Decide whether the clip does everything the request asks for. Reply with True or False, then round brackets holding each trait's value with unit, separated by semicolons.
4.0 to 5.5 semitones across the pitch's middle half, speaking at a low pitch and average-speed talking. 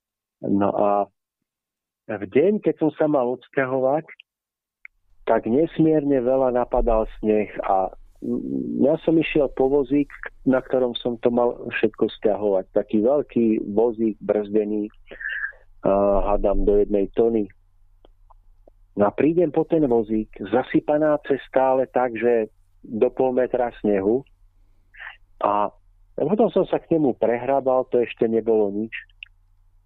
True (4.6 semitones; 115 Hz; 120 wpm)